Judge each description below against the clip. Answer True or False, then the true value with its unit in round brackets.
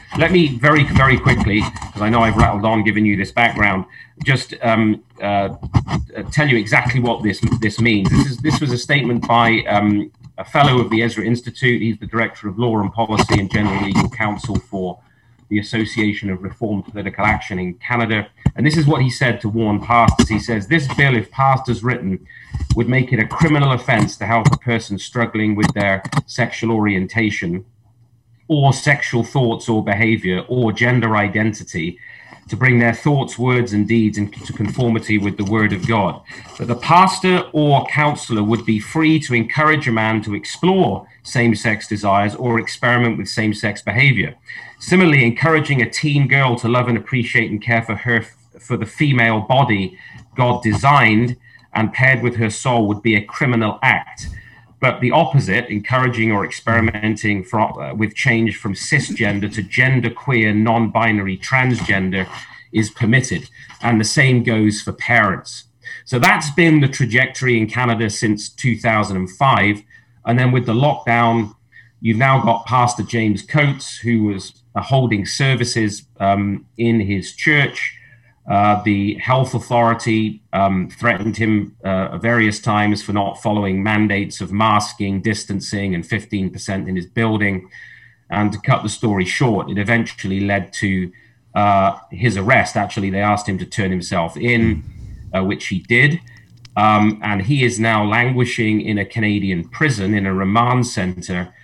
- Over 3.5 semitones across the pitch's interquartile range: False (2.9 semitones)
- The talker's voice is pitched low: True (115 Hz)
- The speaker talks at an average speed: True (165 wpm)